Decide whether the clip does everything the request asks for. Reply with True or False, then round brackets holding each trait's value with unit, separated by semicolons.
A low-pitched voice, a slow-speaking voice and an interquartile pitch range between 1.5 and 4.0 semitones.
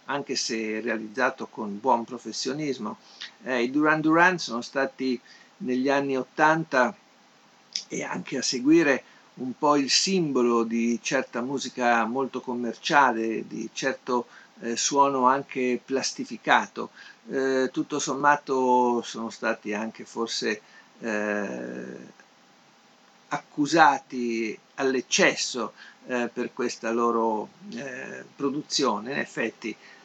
True (125 Hz; 105 wpm; 3.3 semitones)